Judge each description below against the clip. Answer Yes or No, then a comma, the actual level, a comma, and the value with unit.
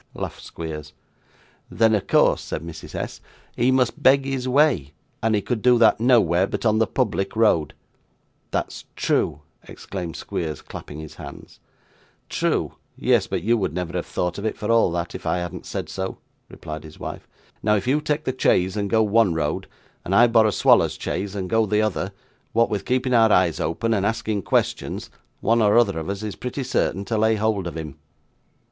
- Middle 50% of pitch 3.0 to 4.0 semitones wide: No, average, 4.5 semitones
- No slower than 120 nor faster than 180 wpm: No, average, 195 wpm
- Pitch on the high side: No, low, 105 Hz